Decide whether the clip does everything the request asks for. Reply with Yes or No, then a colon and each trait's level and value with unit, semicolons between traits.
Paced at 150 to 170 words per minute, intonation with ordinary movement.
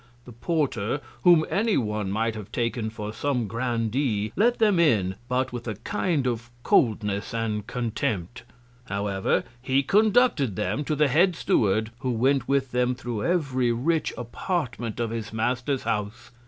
Yes: average, 155 wpm; average, 4.4 semitones